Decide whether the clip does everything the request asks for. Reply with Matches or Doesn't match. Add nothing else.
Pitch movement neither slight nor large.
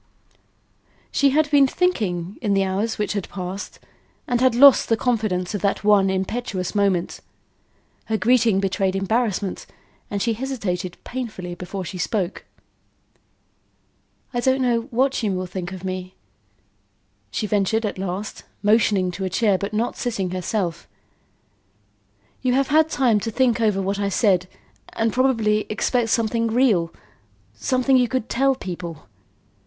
Matches